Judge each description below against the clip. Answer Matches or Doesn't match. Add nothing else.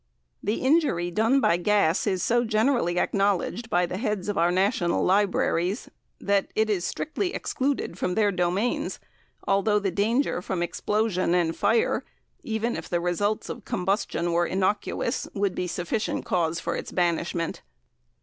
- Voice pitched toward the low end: Doesn't match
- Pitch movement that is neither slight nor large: Matches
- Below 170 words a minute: Matches